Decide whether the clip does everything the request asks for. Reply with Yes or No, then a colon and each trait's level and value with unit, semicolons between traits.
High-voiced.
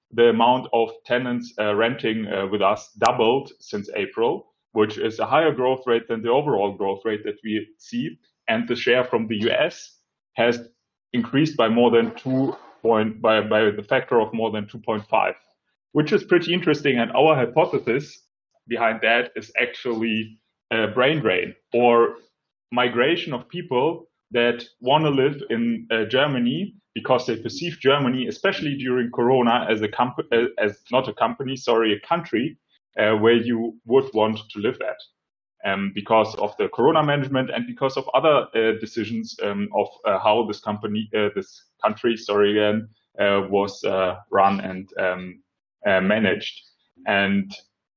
No: low, 115 Hz